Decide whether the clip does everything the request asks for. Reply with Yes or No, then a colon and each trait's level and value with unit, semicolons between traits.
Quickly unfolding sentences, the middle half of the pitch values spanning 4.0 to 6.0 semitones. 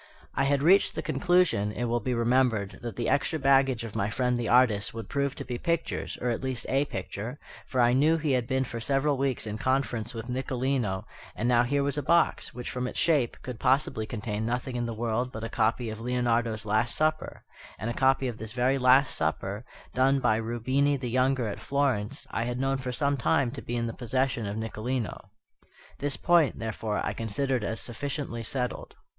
No: fast, 210 wpm; average, 3.0 semitones